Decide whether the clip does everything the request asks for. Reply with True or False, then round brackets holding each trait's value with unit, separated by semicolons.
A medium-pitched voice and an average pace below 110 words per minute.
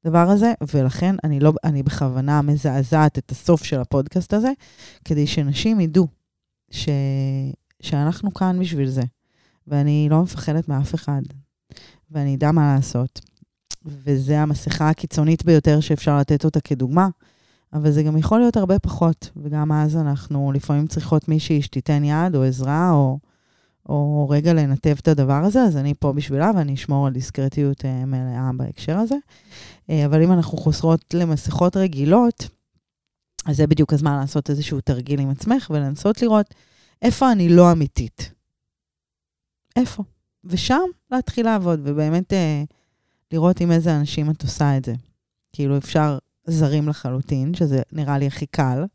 False (150 Hz; 145 wpm)